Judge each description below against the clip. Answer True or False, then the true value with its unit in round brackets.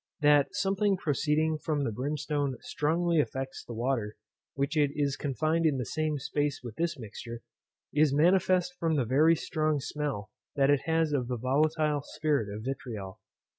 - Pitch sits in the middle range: True (145 Hz)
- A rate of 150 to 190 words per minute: True (160 wpm)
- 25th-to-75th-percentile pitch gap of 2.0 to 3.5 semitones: True (2.9 semitones)